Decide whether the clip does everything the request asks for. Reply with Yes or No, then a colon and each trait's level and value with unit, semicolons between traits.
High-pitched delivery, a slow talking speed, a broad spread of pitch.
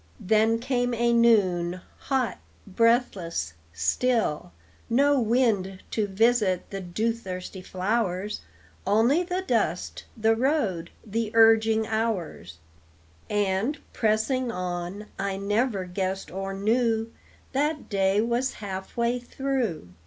No: high, 220 Hz; slow, 110 wpm; average, 3.9 semitones